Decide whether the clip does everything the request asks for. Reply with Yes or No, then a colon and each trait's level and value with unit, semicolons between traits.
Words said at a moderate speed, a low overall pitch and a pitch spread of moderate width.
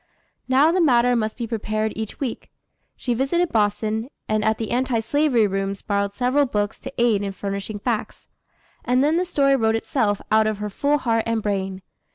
No: average, 190 wpm; high, 225 Hz; average, 3.8 semitones